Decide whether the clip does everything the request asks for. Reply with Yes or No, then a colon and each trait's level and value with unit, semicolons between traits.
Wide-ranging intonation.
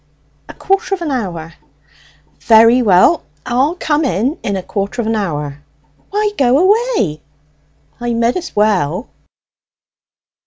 Yes: wide, 8.4 semitones